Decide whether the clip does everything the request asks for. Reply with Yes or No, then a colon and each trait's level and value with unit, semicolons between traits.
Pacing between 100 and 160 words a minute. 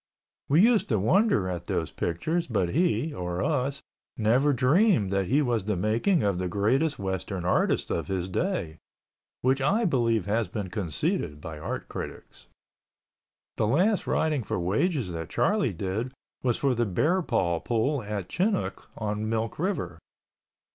Yes: average, 155 wpm